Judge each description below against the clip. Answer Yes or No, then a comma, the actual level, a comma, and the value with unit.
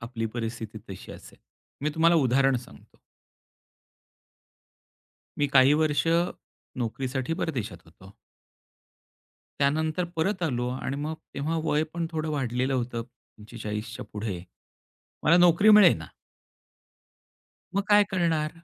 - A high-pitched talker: No, low, 135 Hz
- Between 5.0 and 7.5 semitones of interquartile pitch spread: Yes, wide, 5.5 semitones